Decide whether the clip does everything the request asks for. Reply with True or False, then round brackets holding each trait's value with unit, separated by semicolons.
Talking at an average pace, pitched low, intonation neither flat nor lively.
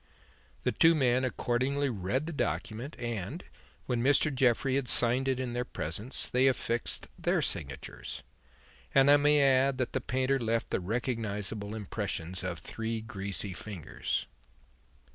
True (145 wpm; 120 Hz; 3.9 semitones)